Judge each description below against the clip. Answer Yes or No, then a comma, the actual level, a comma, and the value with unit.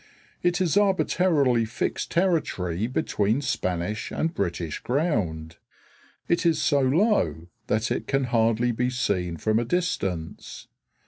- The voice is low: Yes, low, 120 Hz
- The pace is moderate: No, slow, 125 wpm